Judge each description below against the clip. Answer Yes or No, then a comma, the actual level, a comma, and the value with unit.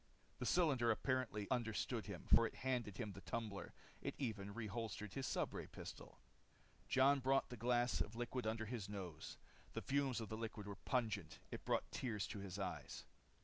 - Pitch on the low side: Yes, low, 115 Hz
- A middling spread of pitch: Yes, average, 3.6 semitones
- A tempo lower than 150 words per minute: No, average, 175 wpm